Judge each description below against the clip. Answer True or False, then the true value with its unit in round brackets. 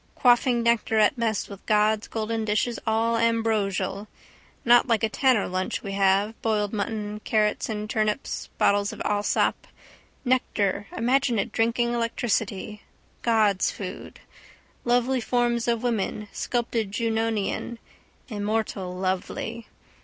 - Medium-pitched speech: False (220 Hz)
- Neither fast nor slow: False (120 wpm)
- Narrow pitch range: True (2.2 semitones)